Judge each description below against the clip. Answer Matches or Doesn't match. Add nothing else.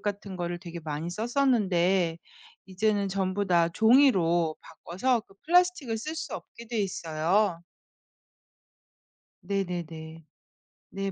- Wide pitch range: Doesn't match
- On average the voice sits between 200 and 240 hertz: Doesn't match